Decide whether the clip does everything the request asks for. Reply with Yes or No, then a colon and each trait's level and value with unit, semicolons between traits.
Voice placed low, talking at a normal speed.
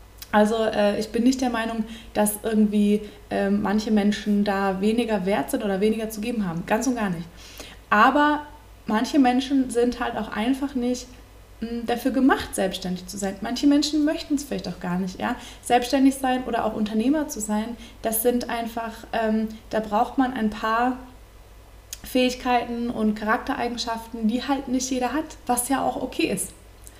No: high, 230 Hz; average, 160 wpm